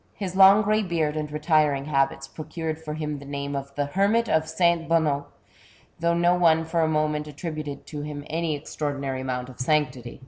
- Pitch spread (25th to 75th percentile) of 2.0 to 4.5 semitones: Yes, average, 2.8 semitones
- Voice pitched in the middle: Yes, medium, 155 Hz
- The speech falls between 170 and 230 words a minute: Yes, average, 195 wpm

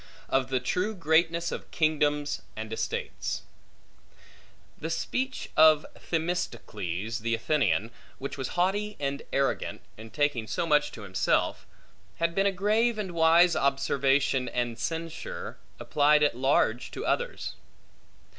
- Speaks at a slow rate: Yes, slow, 125 wpm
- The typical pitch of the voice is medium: Yes, medium, 150 Hz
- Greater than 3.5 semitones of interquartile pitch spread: Yes, average, 5.0 semitones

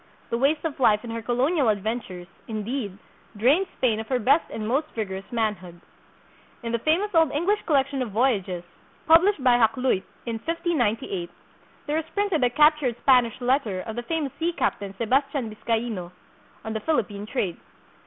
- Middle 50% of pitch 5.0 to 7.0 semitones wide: Yes, wide, 5.4 semitones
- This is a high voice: Yes, high, 245 Hz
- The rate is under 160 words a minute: No, average, 165 wpm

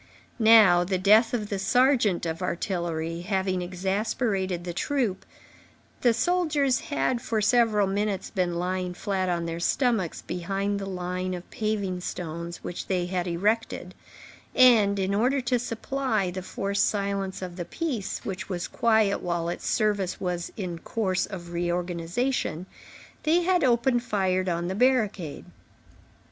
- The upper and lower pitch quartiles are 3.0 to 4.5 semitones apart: Yes, average, 4.2 semitones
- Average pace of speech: Yes, average, 145 wpm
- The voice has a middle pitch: No, high, 195 Hz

